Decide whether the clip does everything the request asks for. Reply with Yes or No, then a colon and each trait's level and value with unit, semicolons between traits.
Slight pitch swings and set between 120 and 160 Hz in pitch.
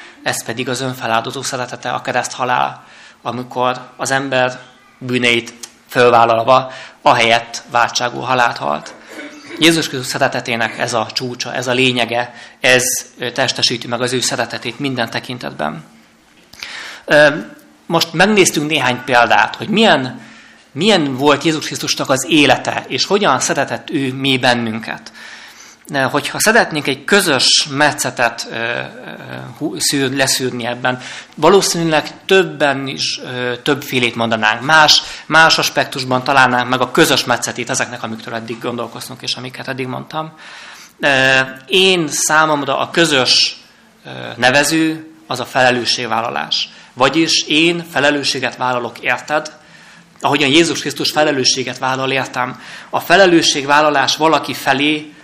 No: average, 3.6 semitones; low, 130 Hz